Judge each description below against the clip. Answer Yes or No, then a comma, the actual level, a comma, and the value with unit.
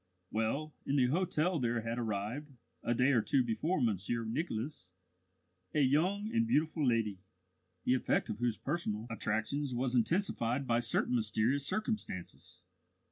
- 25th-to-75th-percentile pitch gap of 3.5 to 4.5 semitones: No, average, 5.1 semitones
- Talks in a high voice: No, low, 125 Hz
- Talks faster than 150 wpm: No, average, 140 wpm